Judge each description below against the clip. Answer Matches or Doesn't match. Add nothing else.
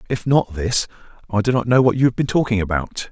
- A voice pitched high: Doesn't match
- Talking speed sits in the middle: Doesn't match